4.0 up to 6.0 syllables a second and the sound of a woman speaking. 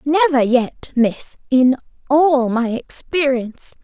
No: 3.5 syllables/s; female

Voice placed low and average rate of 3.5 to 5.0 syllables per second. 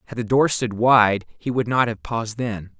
Yes: low, 115 Hz; 4.7 syllables/s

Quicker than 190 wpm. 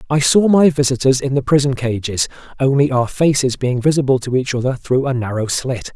Yes: average, 200 wpm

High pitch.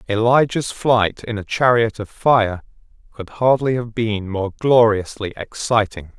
No: low, 110 Hz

